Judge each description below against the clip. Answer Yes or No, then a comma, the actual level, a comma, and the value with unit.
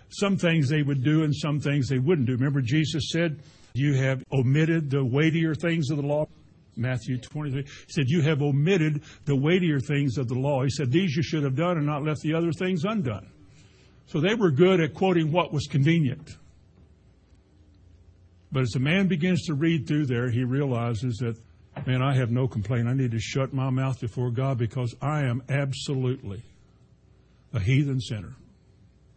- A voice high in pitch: No, medium, 140 Hz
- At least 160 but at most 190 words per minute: Yes, average, 185 wpm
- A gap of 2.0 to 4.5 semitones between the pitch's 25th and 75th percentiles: Yes, average, 3.7 semitones